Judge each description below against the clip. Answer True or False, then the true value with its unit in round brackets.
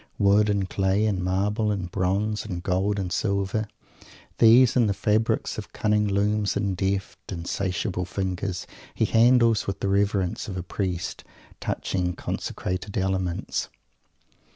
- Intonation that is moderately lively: False (2.2 semitones)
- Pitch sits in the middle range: False (100 Hz)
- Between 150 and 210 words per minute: False (135 wpm)